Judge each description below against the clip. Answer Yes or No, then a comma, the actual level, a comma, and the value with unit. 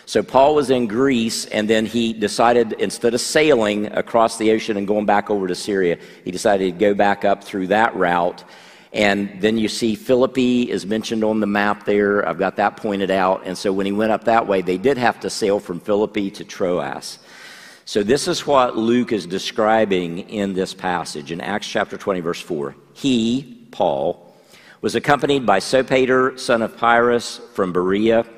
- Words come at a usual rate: Yes, average, 190 wpm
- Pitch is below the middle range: Yes, low, 110 Hz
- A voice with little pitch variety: No, average, 3.0 semitones